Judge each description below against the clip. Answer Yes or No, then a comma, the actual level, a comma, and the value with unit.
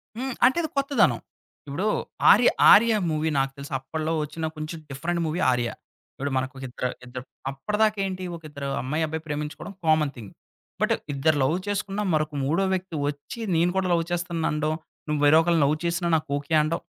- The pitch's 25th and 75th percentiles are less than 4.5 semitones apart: Yes, average, 3.7 semitones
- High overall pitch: No, medium, 155 Hz